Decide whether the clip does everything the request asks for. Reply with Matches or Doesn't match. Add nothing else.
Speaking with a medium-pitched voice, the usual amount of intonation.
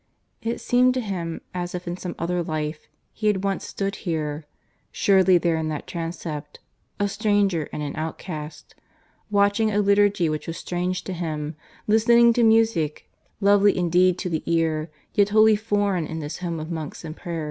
Matches